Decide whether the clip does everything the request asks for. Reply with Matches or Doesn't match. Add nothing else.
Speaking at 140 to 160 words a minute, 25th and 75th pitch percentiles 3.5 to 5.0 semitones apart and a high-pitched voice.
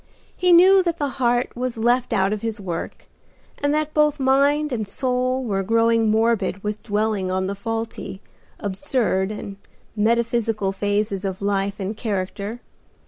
Matches